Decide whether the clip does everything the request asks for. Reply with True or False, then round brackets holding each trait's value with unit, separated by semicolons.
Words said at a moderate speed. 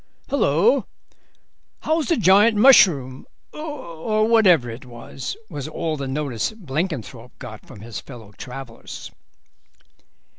False (110 wpm)